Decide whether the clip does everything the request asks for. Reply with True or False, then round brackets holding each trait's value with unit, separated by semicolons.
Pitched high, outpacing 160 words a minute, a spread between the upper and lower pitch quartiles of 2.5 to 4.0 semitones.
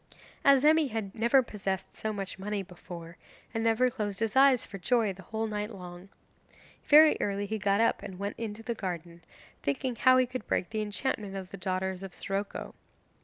True (210 Hz; 185 wpm; 3.3 semitones)